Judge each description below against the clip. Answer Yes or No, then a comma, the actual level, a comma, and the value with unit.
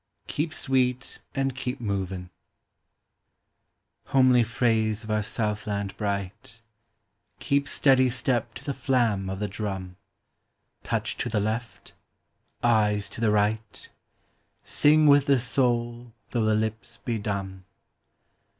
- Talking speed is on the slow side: Yes, slow, 130 wpm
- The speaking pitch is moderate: No, low, 115 Hz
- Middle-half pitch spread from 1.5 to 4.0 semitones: Yes, average, 3.5 semitones